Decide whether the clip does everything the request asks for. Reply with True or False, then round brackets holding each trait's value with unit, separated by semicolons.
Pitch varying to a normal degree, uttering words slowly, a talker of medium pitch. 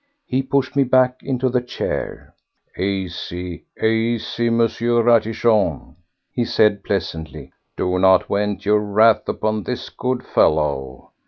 False (4.1 semitones; 120 wpm; 110 Hz)